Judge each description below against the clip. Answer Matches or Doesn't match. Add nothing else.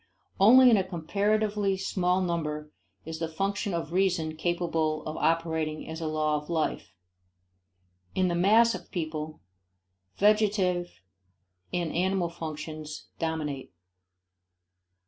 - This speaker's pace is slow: Matches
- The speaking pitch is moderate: Matches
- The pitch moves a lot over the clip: Doesn't match